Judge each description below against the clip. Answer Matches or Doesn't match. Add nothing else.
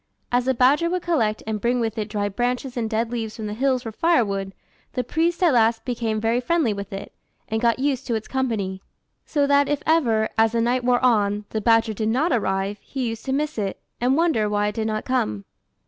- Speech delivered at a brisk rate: Matches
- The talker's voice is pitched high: Matches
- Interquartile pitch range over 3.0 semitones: Matches